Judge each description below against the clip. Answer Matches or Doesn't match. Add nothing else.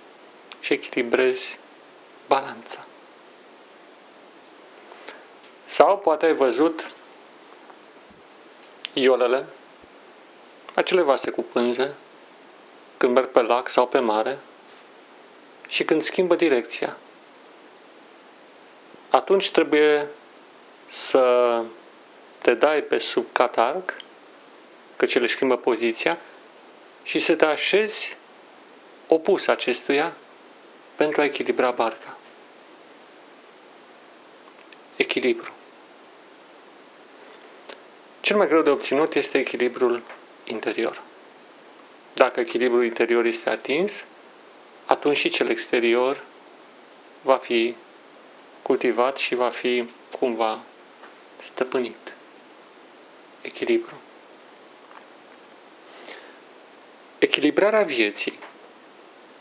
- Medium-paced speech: Doesn't match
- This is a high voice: Doesn't match